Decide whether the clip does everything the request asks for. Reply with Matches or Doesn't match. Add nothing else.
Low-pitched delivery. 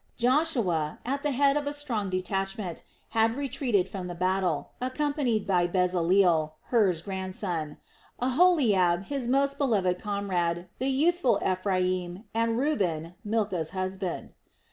Doesn't match